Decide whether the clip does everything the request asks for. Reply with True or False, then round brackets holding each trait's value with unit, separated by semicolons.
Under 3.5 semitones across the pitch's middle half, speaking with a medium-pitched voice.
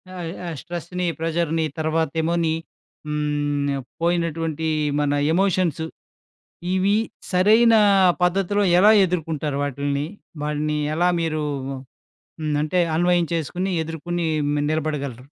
True (2.8 semitones; 165 Hz)